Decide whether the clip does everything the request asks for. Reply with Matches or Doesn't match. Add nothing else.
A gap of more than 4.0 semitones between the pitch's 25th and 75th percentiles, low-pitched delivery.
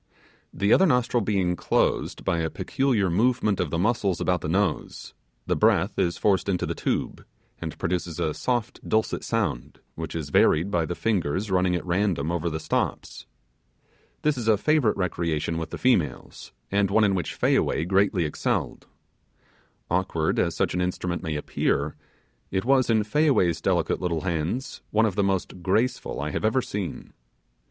Matches